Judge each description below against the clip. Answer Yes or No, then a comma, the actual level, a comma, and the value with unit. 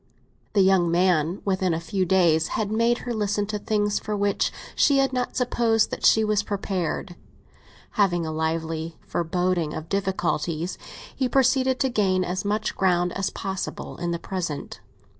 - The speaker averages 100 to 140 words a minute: No, average, 160 wpm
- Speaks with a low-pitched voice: No, high, 190 Hz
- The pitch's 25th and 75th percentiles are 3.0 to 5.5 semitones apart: Yes, average, 3.7 semitones